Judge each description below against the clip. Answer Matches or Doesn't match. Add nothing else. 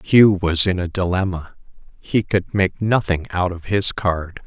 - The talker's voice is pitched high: Doesn't match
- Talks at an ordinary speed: Matches